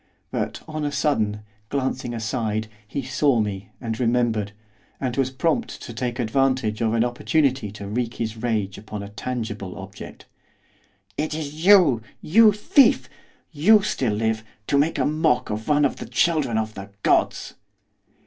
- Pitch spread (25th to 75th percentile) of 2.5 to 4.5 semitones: No, average, 5.1 semitones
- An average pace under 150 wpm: No, average, 160 wpm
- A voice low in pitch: Yes, low, 120 Hz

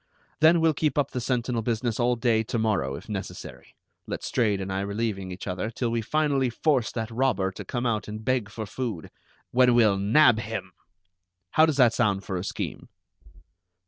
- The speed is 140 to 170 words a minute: No, average, 185 wpm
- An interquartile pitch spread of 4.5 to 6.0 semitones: No, average, 3.7 semitones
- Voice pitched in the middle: No, low, 115 Hz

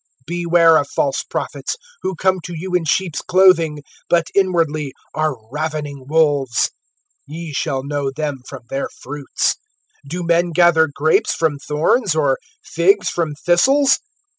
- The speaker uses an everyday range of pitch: Yes, average, 3.1 semitones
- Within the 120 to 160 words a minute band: Yes, average, 140 wpm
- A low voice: No, medium, 160 Hz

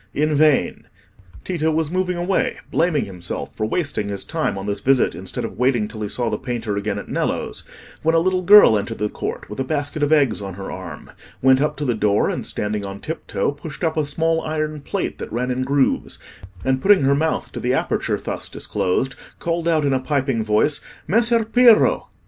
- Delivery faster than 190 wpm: Yes, fast, 205 wpm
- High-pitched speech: No, medium, 140 Hz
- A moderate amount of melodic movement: No, wide, 6.7 semitones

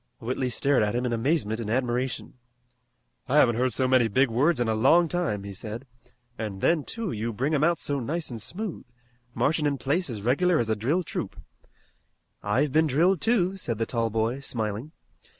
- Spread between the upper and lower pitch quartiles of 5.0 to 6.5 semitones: Yes, wide, 5.5 semitones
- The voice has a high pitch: No, low, 130 Hz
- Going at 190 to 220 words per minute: Yes, average, 195 wpm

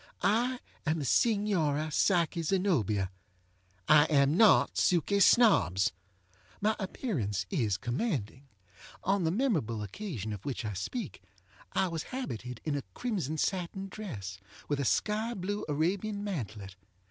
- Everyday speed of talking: No, slow, 130 wpm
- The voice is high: No, medium, 160 Hz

